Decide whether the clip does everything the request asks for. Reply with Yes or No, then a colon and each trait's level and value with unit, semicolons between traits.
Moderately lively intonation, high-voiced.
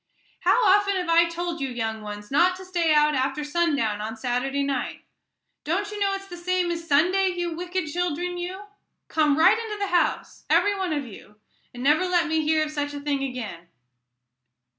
Yes: average, 4.6 semitones; very high, 330 Hz